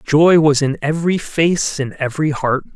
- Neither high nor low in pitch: Yes, medium, 150 Hz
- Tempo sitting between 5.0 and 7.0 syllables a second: No, 4.8 syllables/s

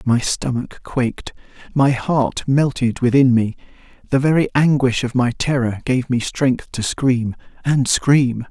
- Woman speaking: No, male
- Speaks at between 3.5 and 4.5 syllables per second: Yes, 4.0 syllables/s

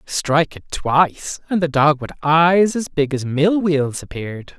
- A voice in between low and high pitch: Yes, medium, 155 Hz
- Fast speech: No, average, 185 wpm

